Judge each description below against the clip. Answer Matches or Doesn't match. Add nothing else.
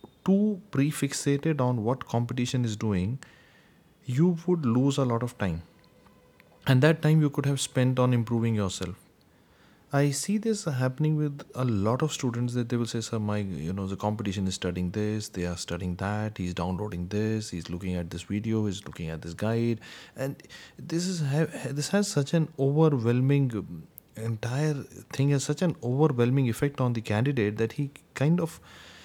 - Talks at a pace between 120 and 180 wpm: Matches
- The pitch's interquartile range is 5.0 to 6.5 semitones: Matches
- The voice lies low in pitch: Matches